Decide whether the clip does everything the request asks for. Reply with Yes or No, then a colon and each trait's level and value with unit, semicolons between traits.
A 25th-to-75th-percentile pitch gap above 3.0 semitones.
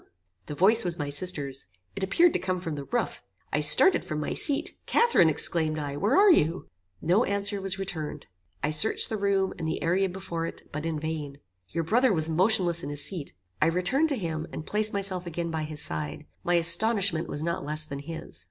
Yes: average, 4.3 semitones